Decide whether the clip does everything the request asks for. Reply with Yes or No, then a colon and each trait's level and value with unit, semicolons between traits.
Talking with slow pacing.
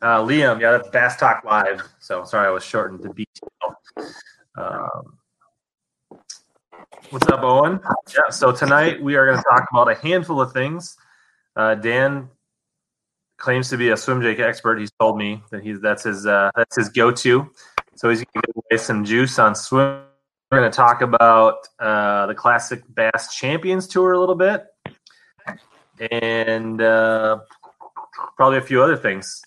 No: average, 165 wpm